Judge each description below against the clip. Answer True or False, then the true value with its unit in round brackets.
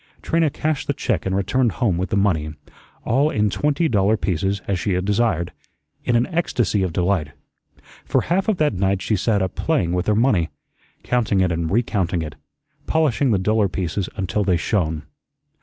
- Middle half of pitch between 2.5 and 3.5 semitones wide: False (5.0 semitones)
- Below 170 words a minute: False (185 wpm)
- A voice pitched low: True (100 Hz)